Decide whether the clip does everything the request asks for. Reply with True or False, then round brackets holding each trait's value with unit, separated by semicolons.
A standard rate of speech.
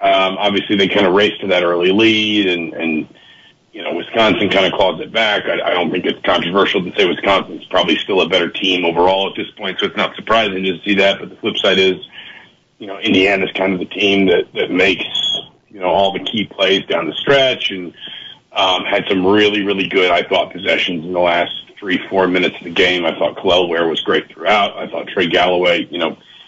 False (230 wpm)